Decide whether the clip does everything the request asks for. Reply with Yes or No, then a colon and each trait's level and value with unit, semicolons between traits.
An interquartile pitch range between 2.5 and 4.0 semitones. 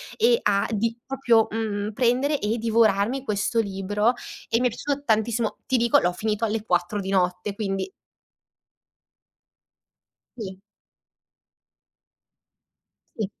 Yes: average, 2.9 semitones